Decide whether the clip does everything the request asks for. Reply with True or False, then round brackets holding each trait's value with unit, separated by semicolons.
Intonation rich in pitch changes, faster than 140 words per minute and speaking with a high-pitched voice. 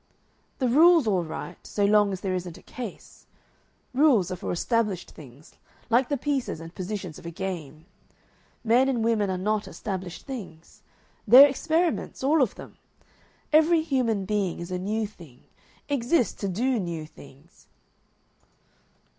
True (6.2 semitones; 150 wpm; 210 Hz)